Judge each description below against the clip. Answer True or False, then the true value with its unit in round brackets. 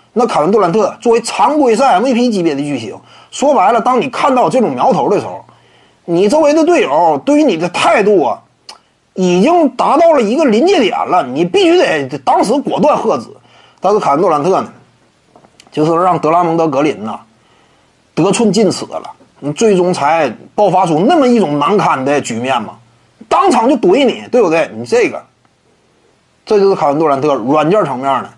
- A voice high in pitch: True (210 Hz)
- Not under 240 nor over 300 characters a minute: True (280 characters per minute)